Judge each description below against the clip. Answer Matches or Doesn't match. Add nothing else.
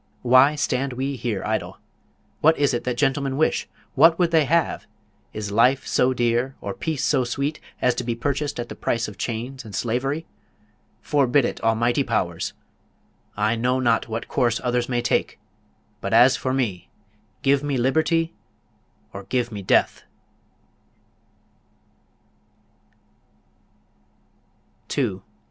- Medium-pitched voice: Doesn't match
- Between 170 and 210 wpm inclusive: Doesn't match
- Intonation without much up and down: Doesn't match